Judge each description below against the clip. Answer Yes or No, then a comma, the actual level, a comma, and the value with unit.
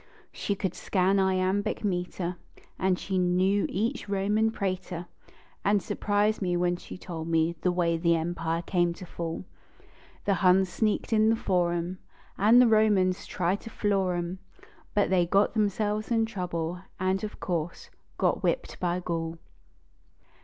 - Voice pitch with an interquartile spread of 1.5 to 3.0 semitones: Yes, average, 2.7 semitones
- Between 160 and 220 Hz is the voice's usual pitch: Yes, medium, 185 Hz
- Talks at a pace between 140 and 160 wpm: Yes, average, 145 wpm